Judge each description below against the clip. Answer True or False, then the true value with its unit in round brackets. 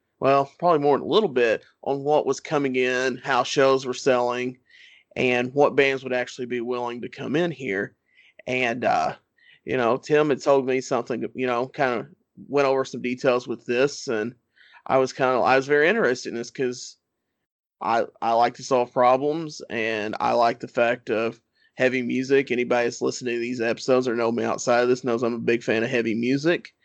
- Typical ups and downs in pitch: False (2.2 semitones)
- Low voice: True (125 Hz)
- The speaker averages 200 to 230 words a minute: True (205 wpm)